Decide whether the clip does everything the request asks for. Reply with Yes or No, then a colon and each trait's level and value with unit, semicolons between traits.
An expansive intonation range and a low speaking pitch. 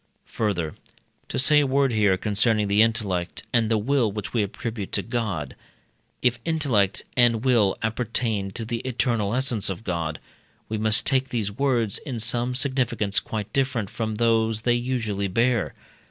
No: average, 3.1 semitones; low, 115 Hz